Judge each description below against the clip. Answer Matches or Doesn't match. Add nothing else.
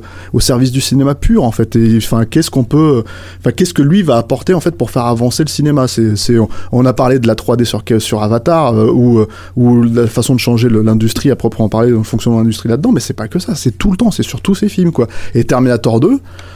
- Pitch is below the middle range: Matches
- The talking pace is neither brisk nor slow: Doesn't match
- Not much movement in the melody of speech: Doesn't match